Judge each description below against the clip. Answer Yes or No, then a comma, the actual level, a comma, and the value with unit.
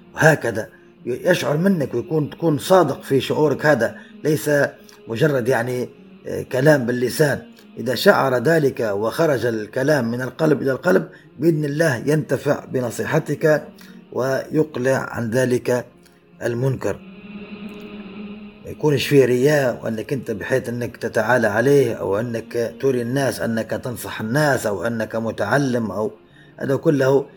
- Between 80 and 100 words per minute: No, average, 115 wpm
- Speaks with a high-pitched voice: No, low, 135 Hz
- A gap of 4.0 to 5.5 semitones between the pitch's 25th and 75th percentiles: Yes, average, 4.7 semitones